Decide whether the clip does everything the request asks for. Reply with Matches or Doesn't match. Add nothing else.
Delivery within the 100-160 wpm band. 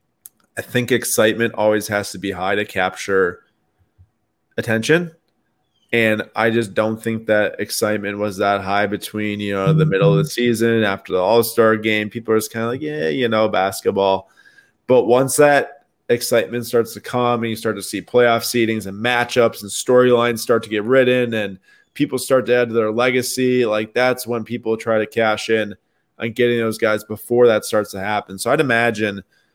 Doesn't match